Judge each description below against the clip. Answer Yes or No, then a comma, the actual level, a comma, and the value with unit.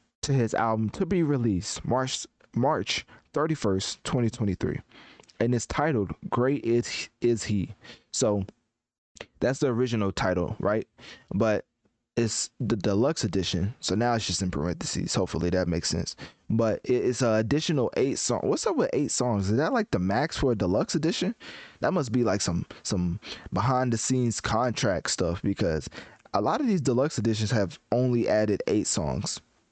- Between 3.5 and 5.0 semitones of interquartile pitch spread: Yes, average, 4.4 semitones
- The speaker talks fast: No, average, 170 wpm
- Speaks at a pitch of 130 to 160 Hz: No, low, 115 Hz